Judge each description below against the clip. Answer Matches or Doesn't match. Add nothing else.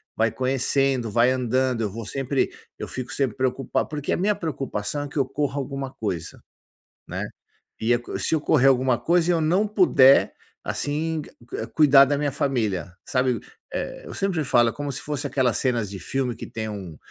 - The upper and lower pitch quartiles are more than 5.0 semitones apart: Doesn't match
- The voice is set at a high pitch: Doesn't match